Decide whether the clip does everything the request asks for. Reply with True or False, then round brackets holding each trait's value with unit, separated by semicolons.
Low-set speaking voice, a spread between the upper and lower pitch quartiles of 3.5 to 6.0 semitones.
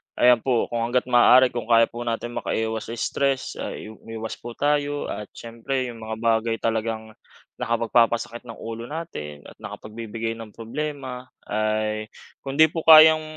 False (115 Hz; 2.4 semitones)